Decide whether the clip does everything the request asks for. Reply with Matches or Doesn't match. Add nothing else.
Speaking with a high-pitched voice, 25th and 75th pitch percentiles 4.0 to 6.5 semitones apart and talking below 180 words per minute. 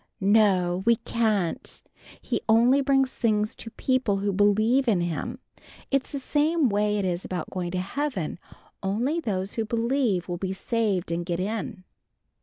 Matches